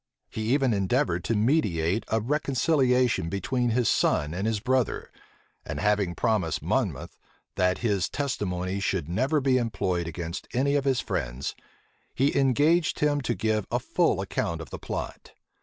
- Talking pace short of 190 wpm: Yes, average, 155 wpm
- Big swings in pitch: Yes, wide, 6.2 semitones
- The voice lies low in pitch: Yes, low, 110 Hz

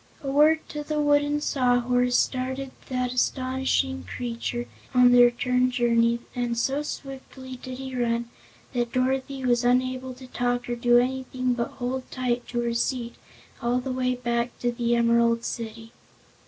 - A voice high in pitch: Yes, very high, 250 Hz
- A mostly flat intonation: Yes, narrow, 1.5 semitones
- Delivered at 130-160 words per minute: Yes, average, 155 wpm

